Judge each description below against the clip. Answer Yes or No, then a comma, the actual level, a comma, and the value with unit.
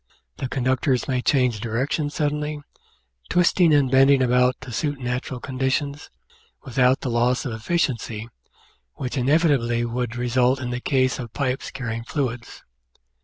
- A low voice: Yes, low, 130 Hz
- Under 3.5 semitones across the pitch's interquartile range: Yes, narrow, 2.4 semitones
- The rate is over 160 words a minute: No, slow, 135 wpm